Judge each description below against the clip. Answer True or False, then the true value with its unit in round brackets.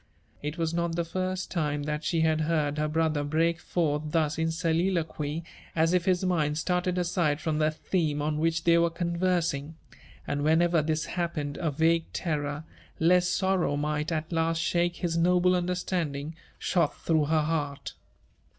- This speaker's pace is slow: False (165 wpm)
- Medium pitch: True (165 Hz)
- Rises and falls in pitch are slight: True (2.2 semitones)